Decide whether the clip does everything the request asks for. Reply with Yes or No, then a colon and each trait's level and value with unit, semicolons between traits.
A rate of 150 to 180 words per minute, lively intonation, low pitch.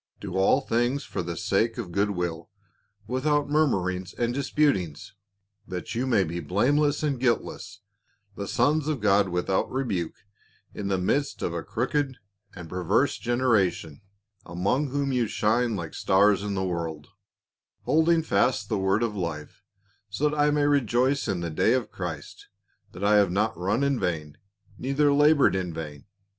Yes: average, 160 wpm; wide, 7.0 semitones; low, 105 Hz